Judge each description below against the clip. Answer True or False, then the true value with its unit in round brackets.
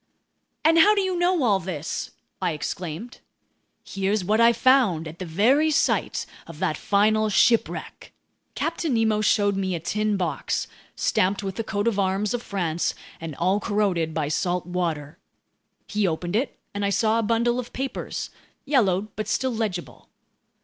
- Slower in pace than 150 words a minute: False (165 wpm)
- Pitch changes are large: False (4.5 semitones)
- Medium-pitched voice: False (205 Hz)